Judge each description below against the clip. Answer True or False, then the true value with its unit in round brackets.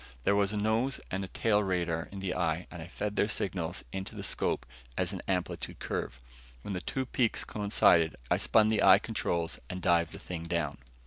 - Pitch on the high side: False (95 Hz)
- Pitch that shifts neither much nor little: True (3.3 semitones)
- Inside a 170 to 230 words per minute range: True (200 wpm)